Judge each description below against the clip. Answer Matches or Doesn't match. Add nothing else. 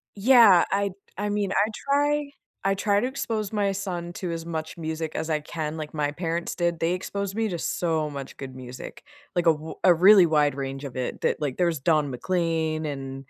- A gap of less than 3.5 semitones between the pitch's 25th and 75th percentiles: Doesn't match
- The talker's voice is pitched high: Doesn't match